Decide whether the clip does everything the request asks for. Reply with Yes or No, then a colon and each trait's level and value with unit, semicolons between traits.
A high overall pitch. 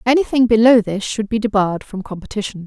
Yes: high, 215 Hz